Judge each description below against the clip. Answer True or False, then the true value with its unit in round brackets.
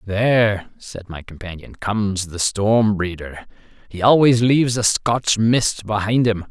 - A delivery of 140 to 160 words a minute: True (150 wpm)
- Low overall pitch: True (105 Hz)